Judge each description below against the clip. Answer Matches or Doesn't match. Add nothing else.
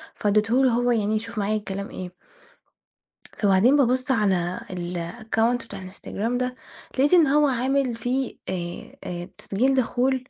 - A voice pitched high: Matches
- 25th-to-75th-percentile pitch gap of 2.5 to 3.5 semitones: Doesn't match